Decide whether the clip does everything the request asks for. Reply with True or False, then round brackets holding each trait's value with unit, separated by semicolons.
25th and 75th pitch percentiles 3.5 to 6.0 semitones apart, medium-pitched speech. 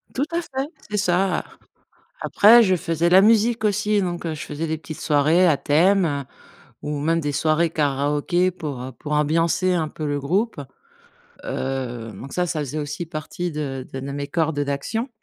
True (4.2 semitones; 160 Hz)